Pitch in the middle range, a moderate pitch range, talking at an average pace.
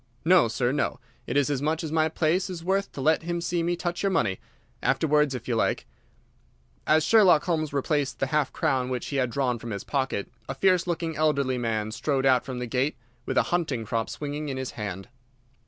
No: medium, 145 Hz; average, 4.4 semitones; fast, 215 wpm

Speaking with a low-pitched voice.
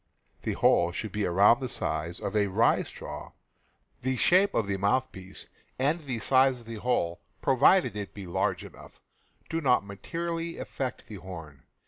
Yes: low, 110 Hz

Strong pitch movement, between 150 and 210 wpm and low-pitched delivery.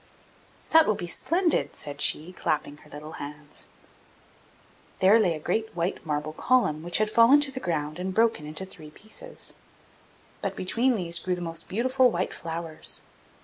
No: wide, 6.7 semitones; average, 165 wpm; medium, 180 Hz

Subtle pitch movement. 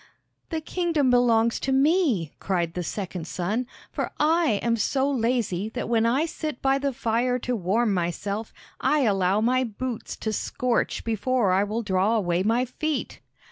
No: average, 4.8 semitones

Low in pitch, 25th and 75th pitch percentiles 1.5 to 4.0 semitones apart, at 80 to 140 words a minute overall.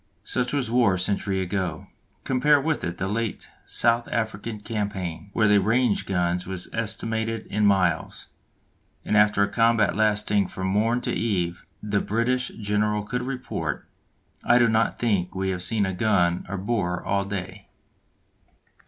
No: low, 105 Hz; average, 3.3 semitones; average, 160 wpm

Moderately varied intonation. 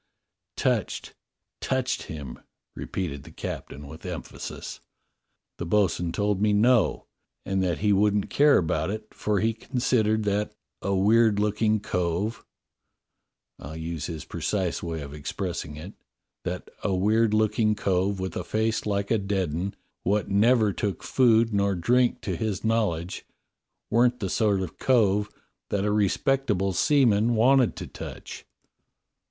Yes: average, 3.3 semitones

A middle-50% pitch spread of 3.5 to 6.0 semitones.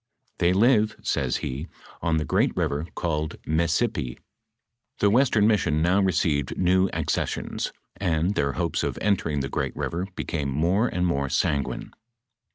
Yes: average, 4.8 semitones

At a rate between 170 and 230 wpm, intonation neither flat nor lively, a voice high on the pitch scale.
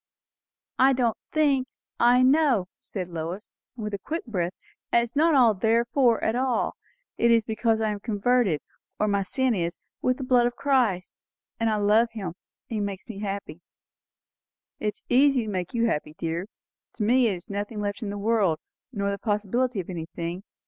Yes: average, 185 wpm; average, 3.8 semitones; high, 220 Hz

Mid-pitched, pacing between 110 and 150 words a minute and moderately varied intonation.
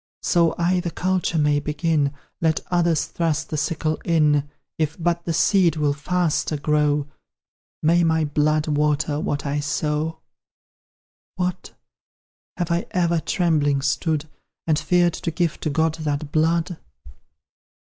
No: medium, 160 Hz; slow, 135 wpm; narrow, 2.3 semitones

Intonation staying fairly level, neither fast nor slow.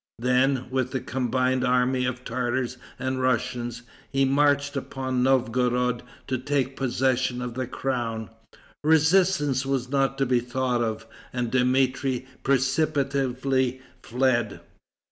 No: narrow, 1.4 semitones; slow, 120 wpm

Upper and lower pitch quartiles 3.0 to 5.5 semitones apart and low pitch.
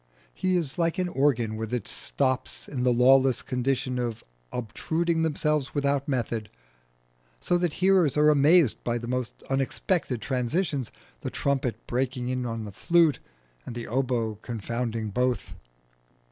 Yes: average, 4.0 semitones; low, 130 Hz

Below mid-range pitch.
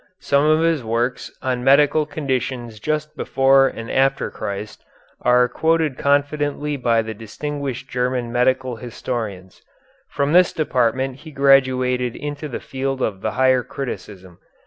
Yes: low, 130 Hz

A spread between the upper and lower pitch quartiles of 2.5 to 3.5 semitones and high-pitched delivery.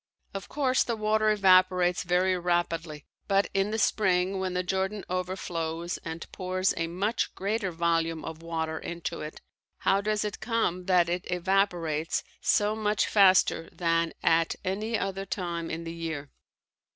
No: average, 2.9 semitones; medium, 180 Hz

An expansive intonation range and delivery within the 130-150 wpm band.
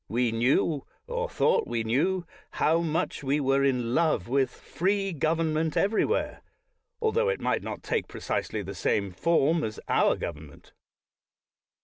Yes: wide, 5.7 semitones; average, 140 wpm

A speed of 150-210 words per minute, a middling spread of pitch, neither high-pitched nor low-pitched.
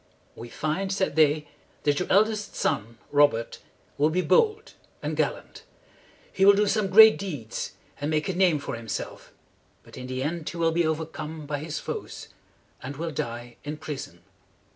Yes: average, 175 wpm; average, 4.8 semitones; medium, 155 Hz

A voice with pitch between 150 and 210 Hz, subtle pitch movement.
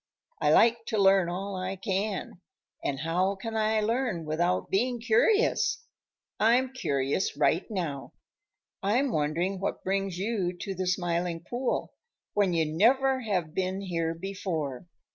No: high, 190 Hz; average, 4.3 semitones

